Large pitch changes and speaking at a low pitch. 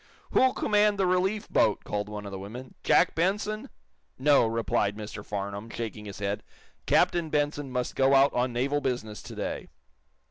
Yes: wide, 8.4 semitones; low, 125 Hz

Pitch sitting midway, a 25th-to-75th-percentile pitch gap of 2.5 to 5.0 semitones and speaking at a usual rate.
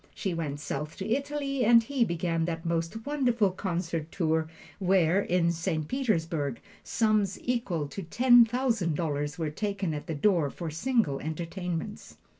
No: medium, 175 Hz; wide, 5.6 semitones; average, 150 wpm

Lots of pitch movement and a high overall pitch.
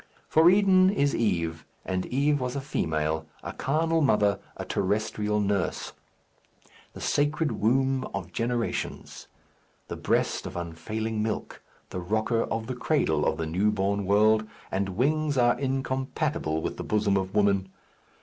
No: wide, 5.7 semitones; low, 110 Hz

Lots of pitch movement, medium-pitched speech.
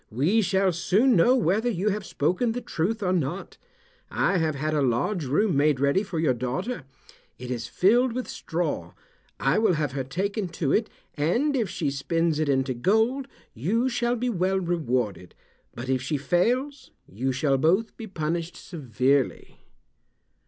Yes: wide, 7.5 semitones; medium, 170 Hz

